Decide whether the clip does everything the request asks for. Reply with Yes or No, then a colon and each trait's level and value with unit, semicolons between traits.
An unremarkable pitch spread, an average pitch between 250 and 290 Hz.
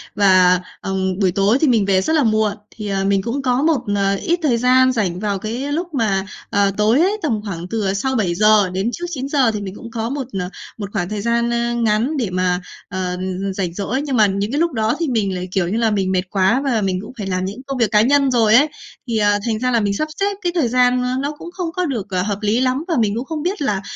No: average, 4.8 semitones; high, 220 Hz